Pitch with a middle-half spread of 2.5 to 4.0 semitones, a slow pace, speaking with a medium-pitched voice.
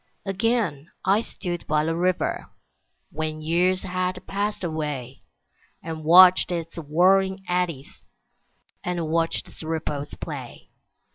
Yes: average, 2.9 semitones; slow, 115 wpm; medium, 170 Hz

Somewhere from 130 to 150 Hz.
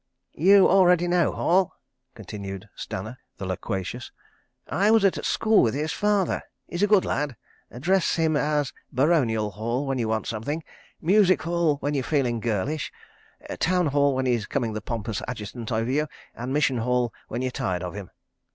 Yes: low, 135 Hz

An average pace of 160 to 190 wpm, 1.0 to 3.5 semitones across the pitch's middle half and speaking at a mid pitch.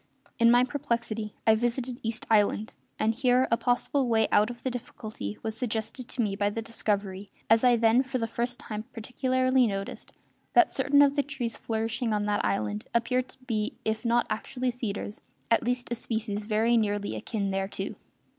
No: average, 185 wpm; narrow, 2.6 semitones; high, 230 Hz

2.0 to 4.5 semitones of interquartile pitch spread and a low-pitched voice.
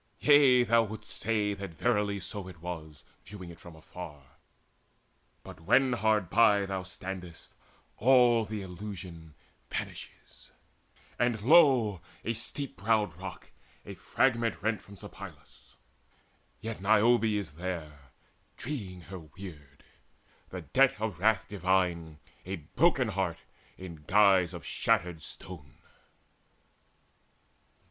Yes: average, 4.1 semitones; low, 100 Hz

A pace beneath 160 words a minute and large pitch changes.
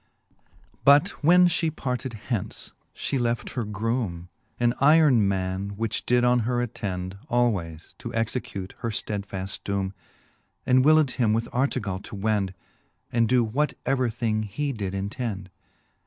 No: average, 145 wpm; average, 4.2 semitones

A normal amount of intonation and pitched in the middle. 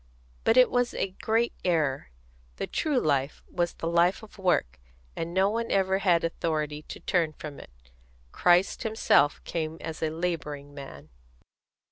Yes: average, 4.2 semitones; medium, 170 Hz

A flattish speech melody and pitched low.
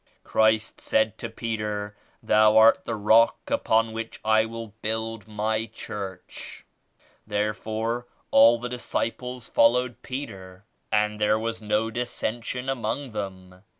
Yes: narrow, 1.4 semitones; low, 110 Hz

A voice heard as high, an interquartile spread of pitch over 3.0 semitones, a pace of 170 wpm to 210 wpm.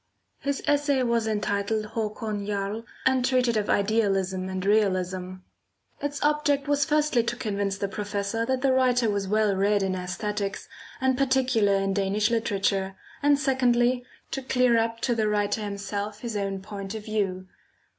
No: high, 215 Hz; average, 4.0 semitones; average, 155 wpm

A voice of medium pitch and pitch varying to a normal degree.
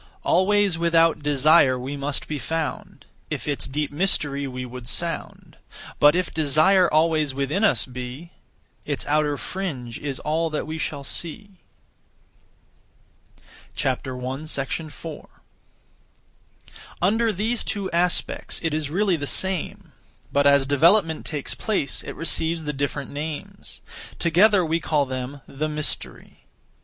Yes: medium, 155 Hz; average, 3.2 semitones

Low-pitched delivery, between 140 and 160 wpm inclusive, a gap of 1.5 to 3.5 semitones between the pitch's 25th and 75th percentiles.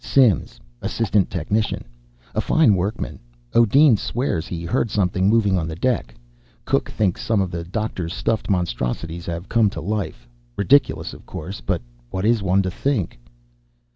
No: very low, 95 Hz; average, 155 wpm; average, 4.6 semitones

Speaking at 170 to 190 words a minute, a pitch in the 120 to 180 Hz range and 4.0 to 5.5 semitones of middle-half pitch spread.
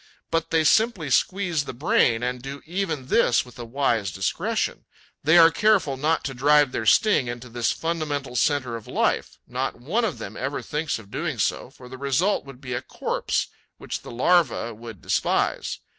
Yes: average, 185 wpm; medium, 140 Hz; average, 5.1 semitones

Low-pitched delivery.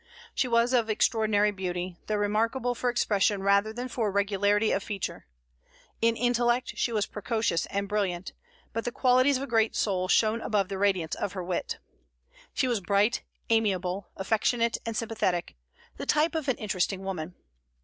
No: high, 210 Hz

